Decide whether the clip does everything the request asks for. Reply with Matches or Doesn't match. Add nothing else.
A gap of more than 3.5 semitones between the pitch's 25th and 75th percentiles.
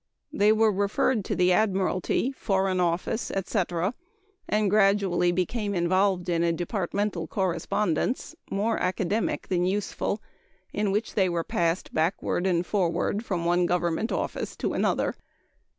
Doesn't match